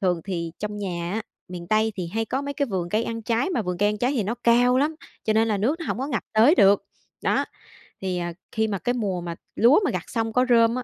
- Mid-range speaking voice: No, high, 220 Hz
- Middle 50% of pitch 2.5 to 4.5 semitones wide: Yes, average, 4.1 semitones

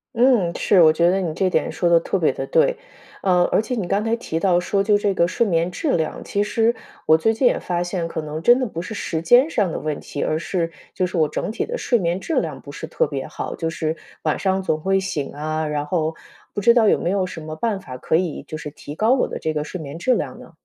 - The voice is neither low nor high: Yes, medium, 180 Hz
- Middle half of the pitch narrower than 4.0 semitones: No, average, 4.7 semitones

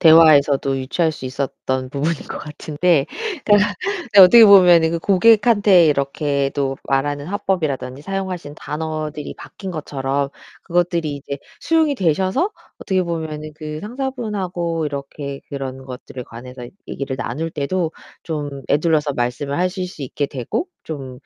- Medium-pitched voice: Yes, medium, 155 Hz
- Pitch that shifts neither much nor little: Yes, average, 4.5 semitones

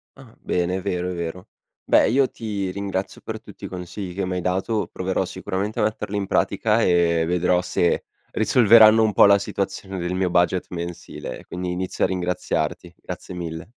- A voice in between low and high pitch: No, very low, 95 Hz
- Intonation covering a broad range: No, narrow, 2.2 semitones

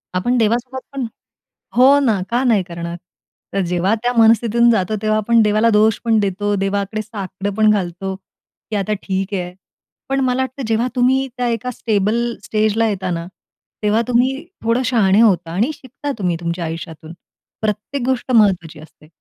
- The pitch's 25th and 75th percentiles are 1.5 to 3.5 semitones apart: No, average, 3.9 semitones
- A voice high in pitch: Yes, high, 215 Hz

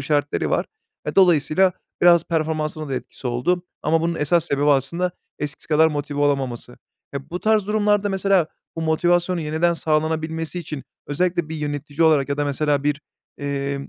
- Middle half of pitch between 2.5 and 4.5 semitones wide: Yes, average, 3.1 semitones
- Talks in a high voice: No, medium, 155 Hz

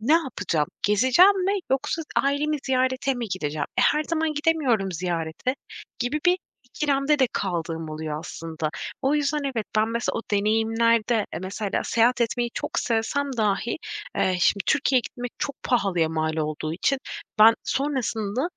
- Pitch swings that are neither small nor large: No, wide, 6.6 semitones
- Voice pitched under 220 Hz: No, high, 230 Hz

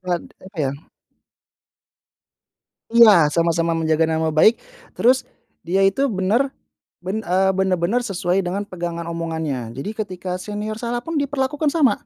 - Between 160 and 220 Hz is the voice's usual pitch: Yes, medium, 185 Hz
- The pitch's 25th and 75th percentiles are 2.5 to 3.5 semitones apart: No, wide, 5.5 semitones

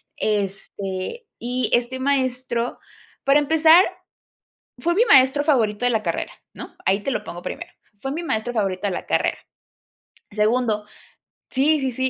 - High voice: Yes, very high, 250 Hz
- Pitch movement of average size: Yes, average, 4.9 semitones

